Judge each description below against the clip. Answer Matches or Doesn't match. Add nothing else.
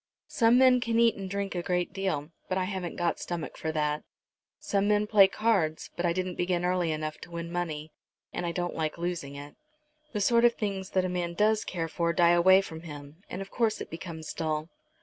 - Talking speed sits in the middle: Doesn't match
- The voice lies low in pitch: Doesn't match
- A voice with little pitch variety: Doesn't match